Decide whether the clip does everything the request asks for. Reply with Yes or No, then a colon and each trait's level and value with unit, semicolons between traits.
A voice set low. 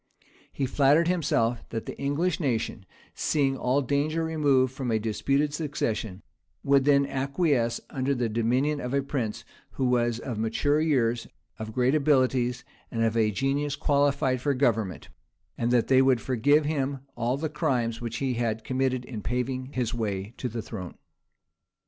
Yes: low, 130 Hz